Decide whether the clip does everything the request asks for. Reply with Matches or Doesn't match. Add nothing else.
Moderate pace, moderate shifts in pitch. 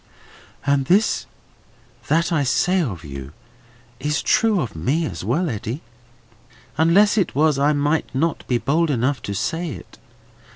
Doesn't match